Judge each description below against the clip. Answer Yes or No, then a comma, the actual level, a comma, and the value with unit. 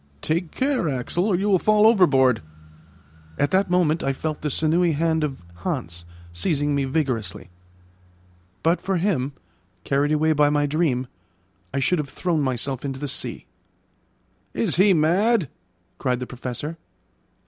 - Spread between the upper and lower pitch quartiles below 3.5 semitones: No, average, 4.7 semitones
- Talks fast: No, average, 150 wpm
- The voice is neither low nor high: Yes, medium, 150 Hz